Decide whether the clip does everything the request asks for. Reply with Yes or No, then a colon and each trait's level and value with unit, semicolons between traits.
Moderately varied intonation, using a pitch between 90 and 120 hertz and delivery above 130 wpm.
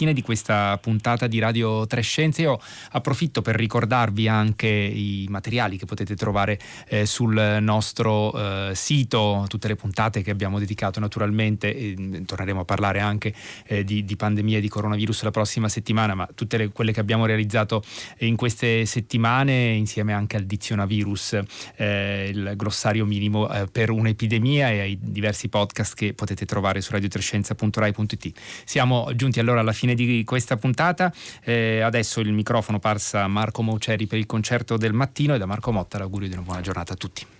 No: narrow, 2.0 semitones; low, 110 Hz; fast, 170 wpm